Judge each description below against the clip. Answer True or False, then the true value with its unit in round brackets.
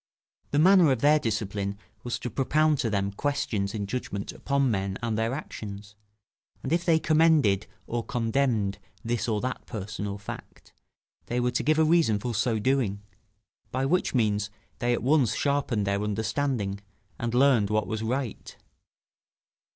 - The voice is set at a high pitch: False (115 Hz)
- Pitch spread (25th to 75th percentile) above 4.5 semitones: True (5.2 semitones)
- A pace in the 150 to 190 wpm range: True (160 wpm)